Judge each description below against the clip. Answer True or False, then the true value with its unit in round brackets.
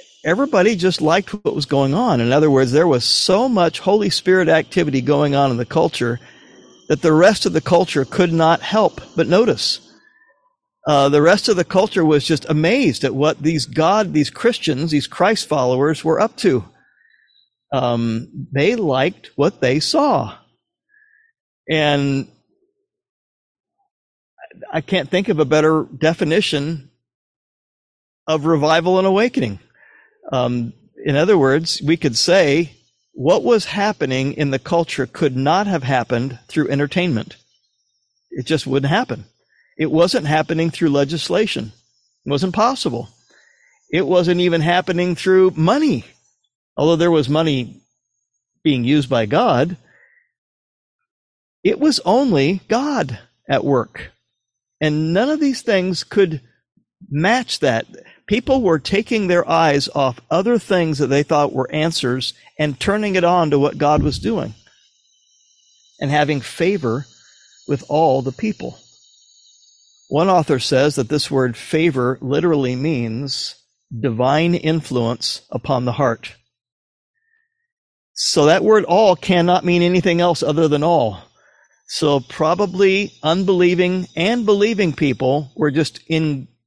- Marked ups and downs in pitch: True (5.7 semitones)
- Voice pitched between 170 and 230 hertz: False (160 Hz)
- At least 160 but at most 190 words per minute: False (135 wpm)